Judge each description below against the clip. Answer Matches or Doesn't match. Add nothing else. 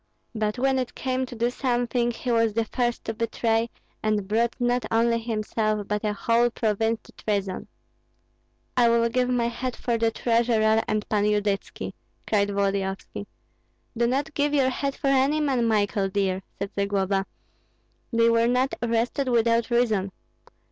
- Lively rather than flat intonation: Doesn't match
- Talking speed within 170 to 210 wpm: Doesn't match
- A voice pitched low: Doesn't match